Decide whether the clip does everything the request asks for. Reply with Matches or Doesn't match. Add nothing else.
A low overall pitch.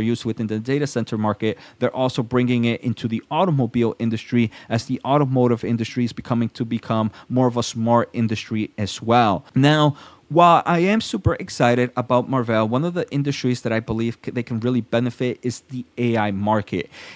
Matches